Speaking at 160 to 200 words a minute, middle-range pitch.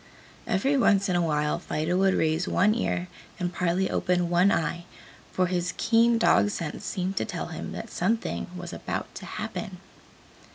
Yes: average, 170 wpm; medium, 180 Hz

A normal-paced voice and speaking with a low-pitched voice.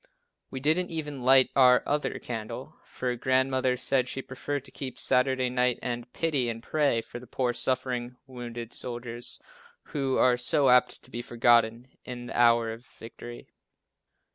Yes: average, 160 wpm; low, 125 Hz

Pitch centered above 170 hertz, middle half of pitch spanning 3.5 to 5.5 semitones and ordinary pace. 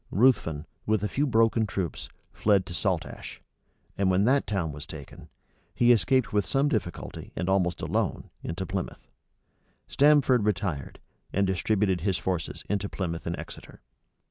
No: low, 100 Hz; average, 4.1 semitones; average, 145 wpm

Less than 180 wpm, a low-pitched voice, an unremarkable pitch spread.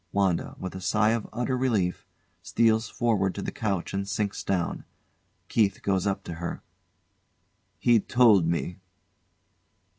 Yes: average, 140 wpm; low, 100 Hz; average, 3.3 semitones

